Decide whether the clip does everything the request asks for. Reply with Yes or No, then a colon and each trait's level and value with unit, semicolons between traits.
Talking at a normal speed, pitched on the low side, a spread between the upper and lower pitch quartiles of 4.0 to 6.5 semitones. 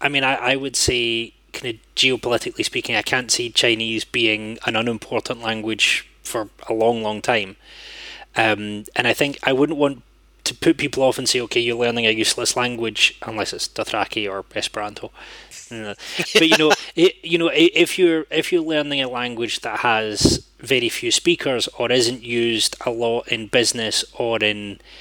Yes: average, 180 wpm; low, 120 Hz; average, 4.4 semitones